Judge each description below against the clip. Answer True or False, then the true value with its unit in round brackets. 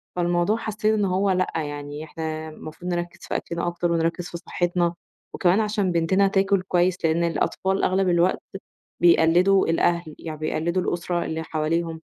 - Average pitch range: False (2.2 semitones)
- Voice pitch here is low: False (175 Hz)